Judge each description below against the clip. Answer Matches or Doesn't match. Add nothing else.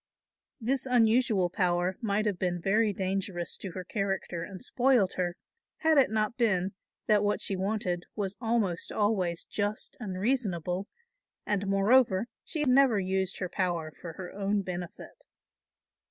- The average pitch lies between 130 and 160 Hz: Doesn't match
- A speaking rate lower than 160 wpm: Matches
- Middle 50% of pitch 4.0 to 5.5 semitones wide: Doesn't match